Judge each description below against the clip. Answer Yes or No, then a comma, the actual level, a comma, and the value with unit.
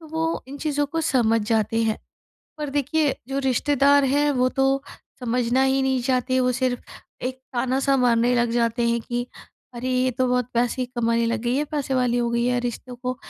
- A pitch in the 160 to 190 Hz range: No, very high, 255 Hz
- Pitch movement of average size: No, narrow, 2.3 semitones